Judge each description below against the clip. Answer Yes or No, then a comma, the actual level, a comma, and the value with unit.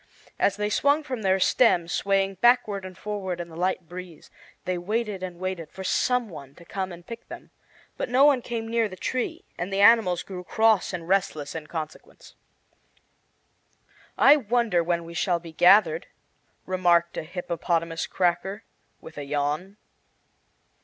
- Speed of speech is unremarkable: Yes, average, 160 wpm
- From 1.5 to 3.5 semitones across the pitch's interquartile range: No, average, 3.9 semitones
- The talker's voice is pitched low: No, medium, 185 Hz